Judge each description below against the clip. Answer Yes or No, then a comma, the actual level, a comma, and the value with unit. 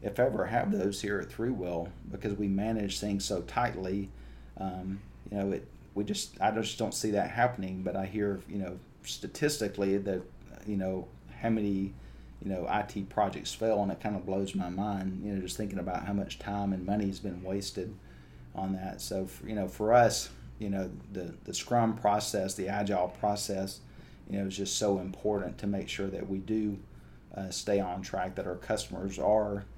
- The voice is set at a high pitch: No, low, 100 Hz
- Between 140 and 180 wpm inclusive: No, average, 195 wpm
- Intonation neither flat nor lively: No, narrow, 1.5 semitones